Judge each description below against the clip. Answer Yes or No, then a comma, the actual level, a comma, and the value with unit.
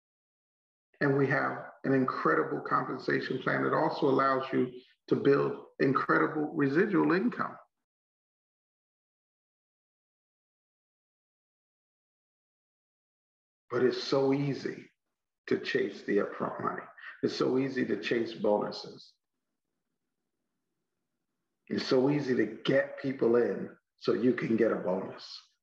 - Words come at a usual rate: No, slow, 105 wpm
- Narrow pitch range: Yes, narrow, 1.7 semitones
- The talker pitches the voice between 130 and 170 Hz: Yes, low, 135 Hz